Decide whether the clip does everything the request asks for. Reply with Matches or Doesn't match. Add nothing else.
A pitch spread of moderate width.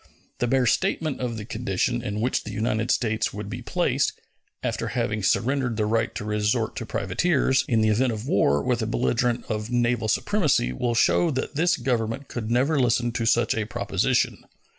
Matches